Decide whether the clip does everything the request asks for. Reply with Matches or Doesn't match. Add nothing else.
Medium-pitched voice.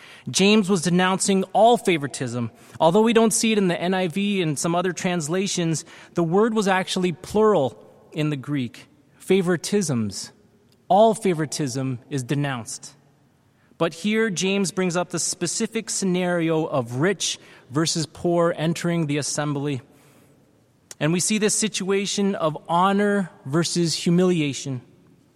Matches